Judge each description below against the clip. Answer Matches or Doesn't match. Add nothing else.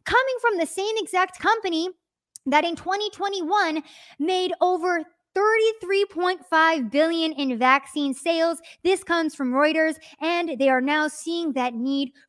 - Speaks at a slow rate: Matches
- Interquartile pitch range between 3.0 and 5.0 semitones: Matches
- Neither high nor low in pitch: Doesn't match